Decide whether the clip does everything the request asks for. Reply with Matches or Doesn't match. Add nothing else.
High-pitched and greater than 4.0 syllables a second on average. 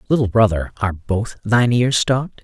Doesn't match